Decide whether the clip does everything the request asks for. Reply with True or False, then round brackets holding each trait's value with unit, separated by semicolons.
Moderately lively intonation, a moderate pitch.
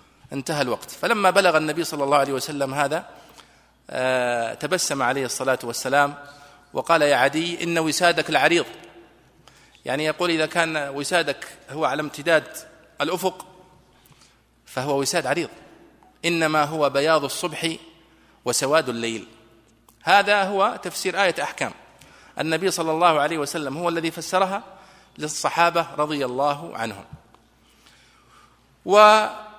True (3.8 semitones; 155 Hz)